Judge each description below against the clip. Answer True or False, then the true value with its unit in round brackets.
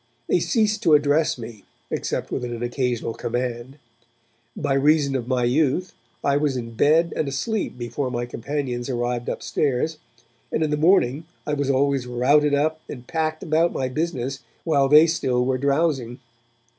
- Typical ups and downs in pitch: True (3.9 semitones)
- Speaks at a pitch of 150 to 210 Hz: False (140 Hz)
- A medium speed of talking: True (160 wpm)